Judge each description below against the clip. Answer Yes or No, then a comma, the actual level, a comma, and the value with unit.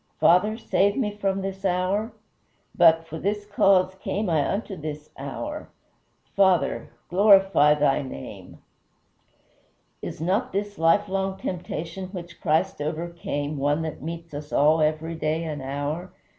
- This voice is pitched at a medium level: Yes, medium, 170 Hz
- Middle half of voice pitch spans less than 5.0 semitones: Yes, average, 4.1 semitones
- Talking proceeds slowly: Yes, slow, 130 wpm